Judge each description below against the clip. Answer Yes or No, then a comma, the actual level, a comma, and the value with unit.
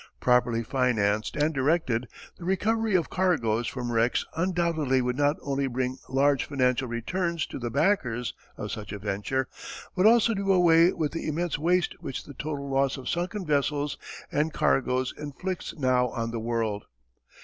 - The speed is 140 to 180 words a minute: Yes, average, 160 wpm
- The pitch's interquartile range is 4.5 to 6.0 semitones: Yes, wide, 5.4 semitones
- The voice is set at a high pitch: No, medium, 140 Hz